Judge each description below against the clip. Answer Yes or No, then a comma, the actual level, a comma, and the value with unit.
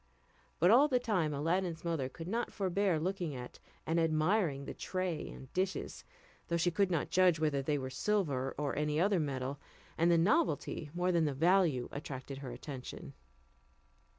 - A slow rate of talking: No, average, 170 wpm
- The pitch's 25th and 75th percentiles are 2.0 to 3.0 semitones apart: No, average, 4.6 semitones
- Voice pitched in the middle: Yes, medium, 165 Hz